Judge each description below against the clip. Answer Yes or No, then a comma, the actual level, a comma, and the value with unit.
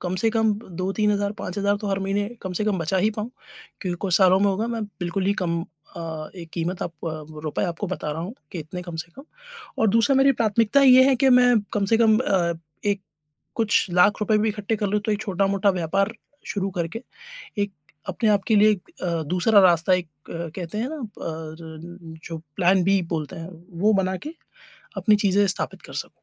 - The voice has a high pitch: Yes, high, 195 Hz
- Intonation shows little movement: No, average, 3.6 semitones